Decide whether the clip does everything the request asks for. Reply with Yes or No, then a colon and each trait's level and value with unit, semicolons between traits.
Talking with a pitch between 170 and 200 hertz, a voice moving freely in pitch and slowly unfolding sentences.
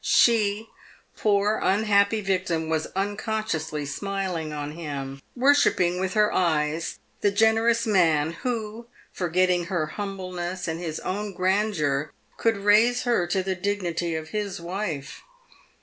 No: high, 190 Hz; average, 4.3 semitones; slow, 125 wpm